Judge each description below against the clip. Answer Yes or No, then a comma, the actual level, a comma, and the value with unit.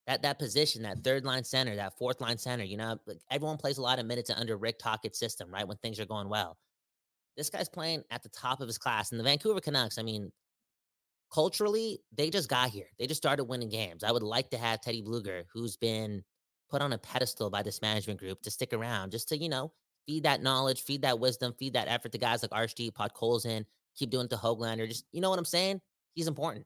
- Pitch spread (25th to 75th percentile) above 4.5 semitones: No, average, 3.7 semitones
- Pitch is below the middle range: Yes, low, 120 Hz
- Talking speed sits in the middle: No, fast, 240 wpm